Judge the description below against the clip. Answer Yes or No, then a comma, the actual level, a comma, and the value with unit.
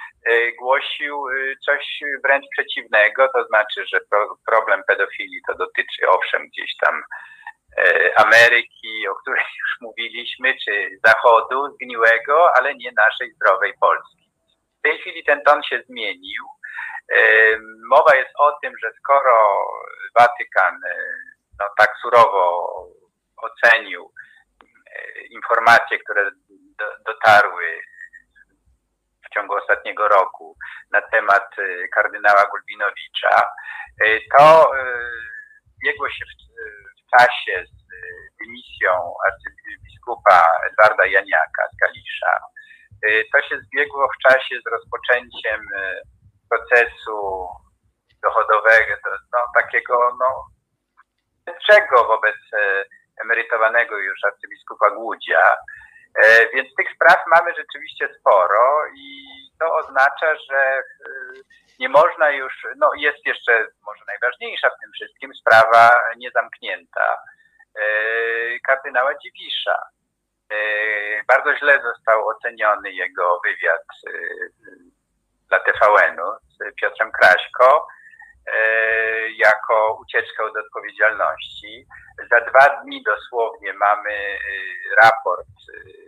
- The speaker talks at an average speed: No, slow, 95 wpm